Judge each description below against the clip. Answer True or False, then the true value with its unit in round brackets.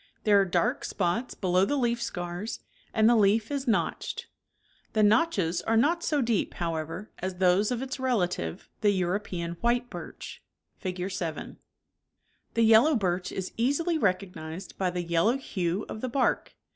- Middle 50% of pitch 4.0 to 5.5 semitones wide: True (4.9 semitones)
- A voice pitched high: True (200 Hz)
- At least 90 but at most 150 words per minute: False (165 wpm)